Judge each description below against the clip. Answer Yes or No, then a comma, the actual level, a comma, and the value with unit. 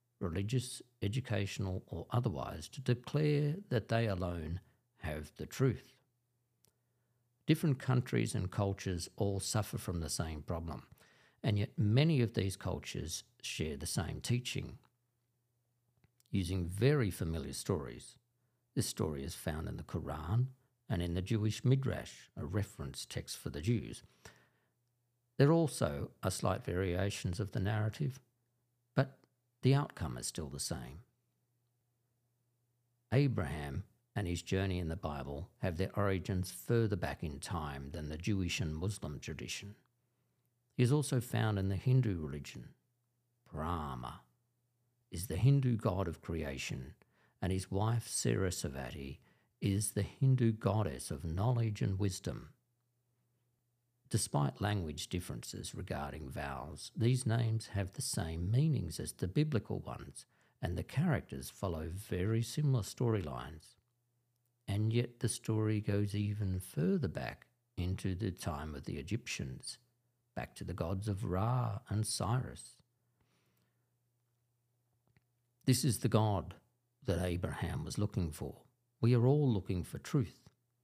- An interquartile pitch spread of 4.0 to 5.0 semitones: Yes, average, 4.7 semitones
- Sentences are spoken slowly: Yes, slow, 130 wpm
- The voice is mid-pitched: No, low, 110 Hz